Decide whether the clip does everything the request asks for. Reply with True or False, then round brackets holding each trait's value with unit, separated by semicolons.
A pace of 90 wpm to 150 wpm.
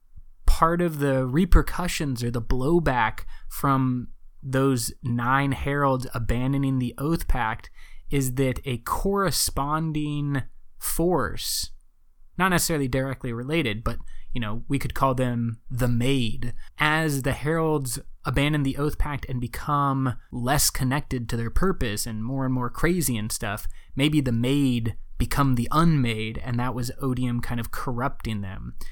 True (140 wpm)